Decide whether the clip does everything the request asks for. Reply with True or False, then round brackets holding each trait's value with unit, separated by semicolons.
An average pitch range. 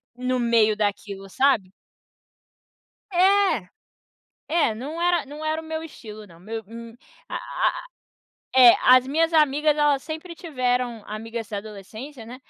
False (6.0 semitones)